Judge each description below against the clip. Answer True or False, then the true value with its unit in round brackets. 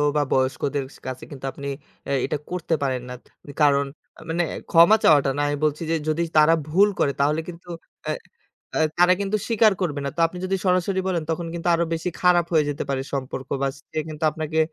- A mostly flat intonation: False (3.7 semitones)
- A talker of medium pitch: True (160 Hz)